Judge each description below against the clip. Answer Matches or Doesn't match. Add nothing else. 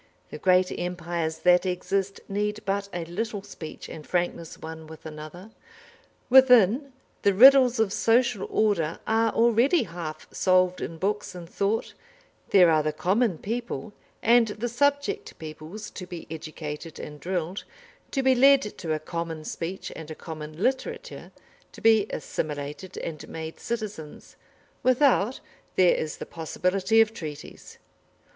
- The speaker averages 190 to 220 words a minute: Doesn't match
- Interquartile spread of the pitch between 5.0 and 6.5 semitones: Matches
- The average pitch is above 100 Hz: Matches